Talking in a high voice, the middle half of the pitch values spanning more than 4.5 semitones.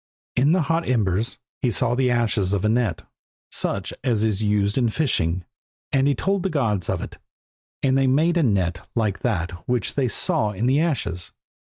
No: low, 115 Hz; average, 5.1 semitones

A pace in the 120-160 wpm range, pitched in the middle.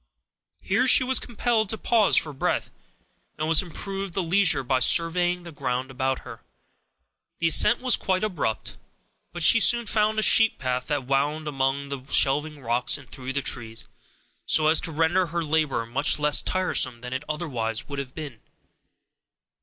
No: average, 170 wpm; medium, 155 Hz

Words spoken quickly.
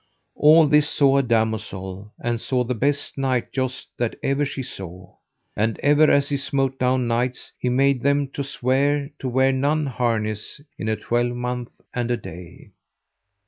No: average, 165 wpm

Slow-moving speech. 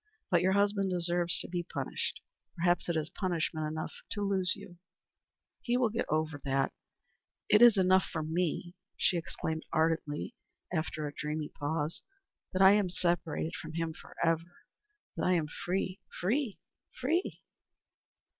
No: average, 145 wpm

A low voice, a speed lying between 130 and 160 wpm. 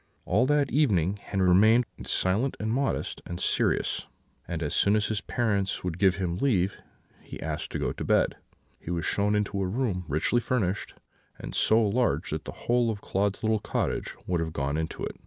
No: low, 100 Hz; average, 190 wpm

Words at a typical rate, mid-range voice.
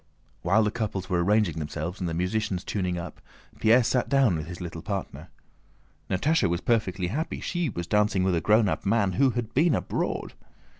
No: average, 190 wpm; low, 100 Hz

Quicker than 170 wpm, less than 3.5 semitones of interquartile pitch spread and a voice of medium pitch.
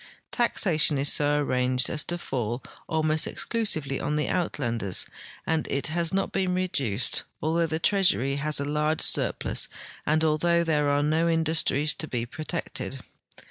No: average, 160 wpm; average, 3.0 semitones; medium, 155 Hz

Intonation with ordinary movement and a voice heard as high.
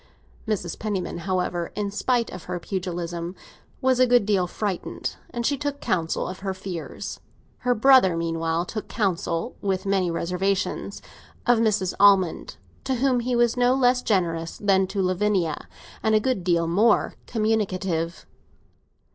Yes: average, 4.4 semitones; high, 195 Hz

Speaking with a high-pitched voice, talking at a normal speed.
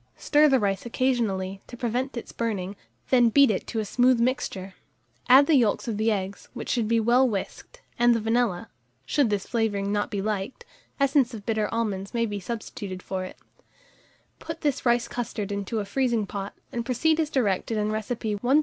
Yes: high, 230 Hz; average, 190 wpm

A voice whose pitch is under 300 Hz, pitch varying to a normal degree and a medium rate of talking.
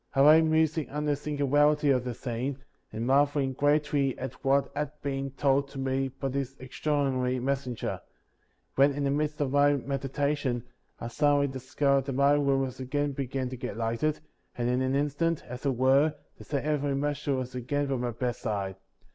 No: low, 135 Hz; narrow, 1.9 semitones; average, 185 wpm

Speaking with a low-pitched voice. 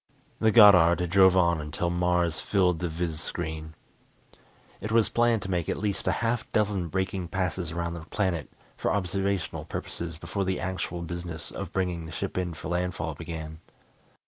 Yes: very low, 90 Hz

